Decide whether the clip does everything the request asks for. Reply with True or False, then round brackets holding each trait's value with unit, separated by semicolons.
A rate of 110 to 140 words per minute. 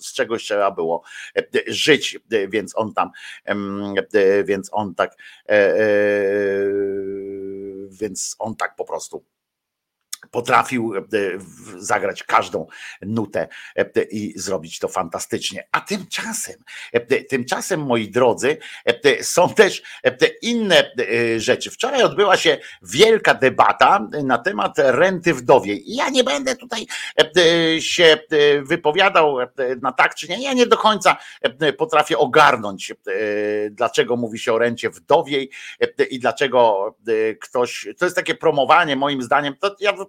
True (120 wpm)